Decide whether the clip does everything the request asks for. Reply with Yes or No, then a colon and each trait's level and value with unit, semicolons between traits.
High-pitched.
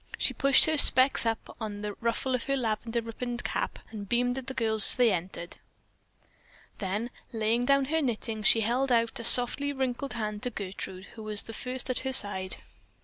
Yes: high, 230 Hz